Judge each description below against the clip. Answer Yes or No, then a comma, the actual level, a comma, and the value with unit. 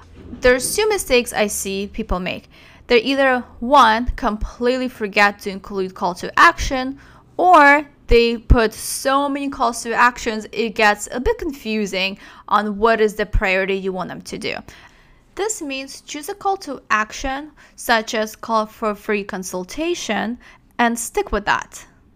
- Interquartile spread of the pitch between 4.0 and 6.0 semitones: Yes, average, 4.6 semitones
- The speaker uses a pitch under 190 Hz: No, high, 230 Hz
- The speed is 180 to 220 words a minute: No, average, 155 wpm